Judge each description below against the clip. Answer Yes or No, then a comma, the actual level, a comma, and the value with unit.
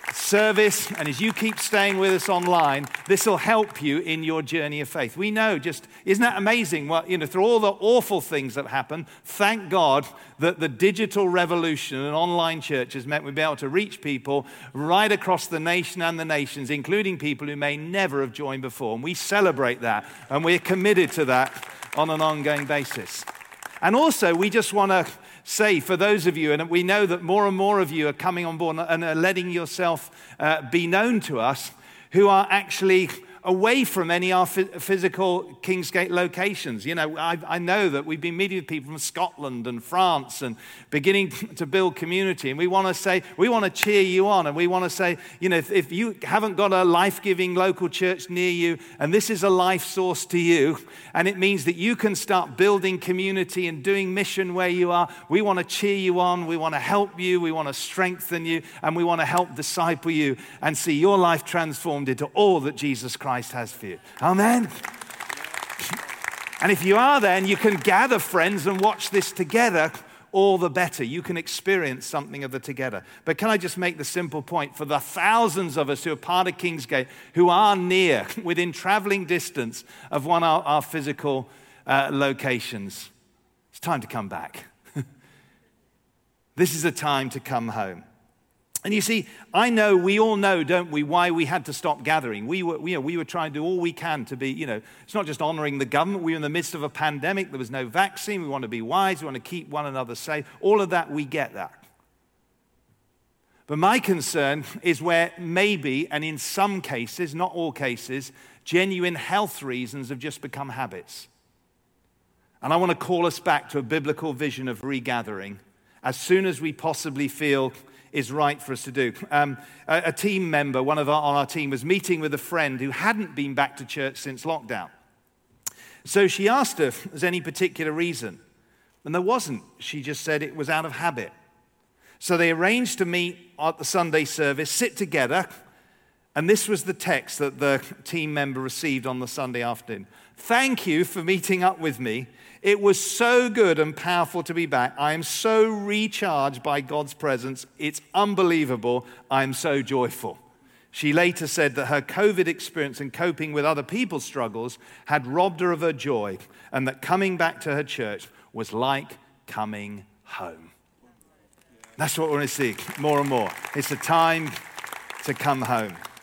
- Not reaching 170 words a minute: No, average, 200 wpm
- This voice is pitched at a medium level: Yes, medium, 165 Hz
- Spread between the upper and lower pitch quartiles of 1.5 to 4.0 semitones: No, average, 4.5 semitones